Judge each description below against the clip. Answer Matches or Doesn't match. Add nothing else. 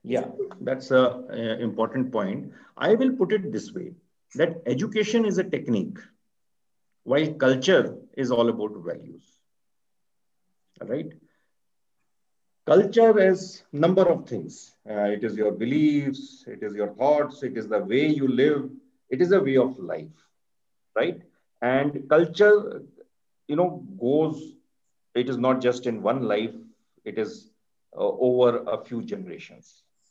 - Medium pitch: Matches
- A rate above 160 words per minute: Doesn't match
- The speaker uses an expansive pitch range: Matches